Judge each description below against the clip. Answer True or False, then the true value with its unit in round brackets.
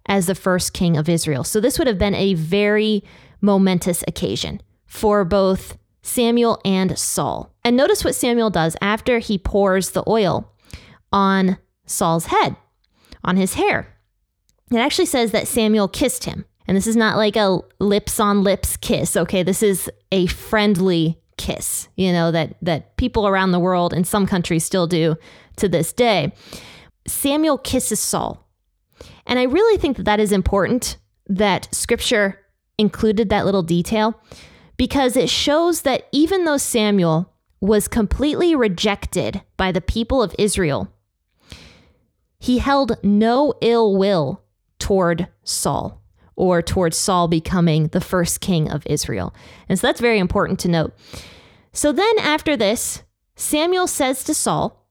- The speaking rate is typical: True (150 wpm)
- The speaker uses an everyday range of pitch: True (4.7 semitones)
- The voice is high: True (200 Hz)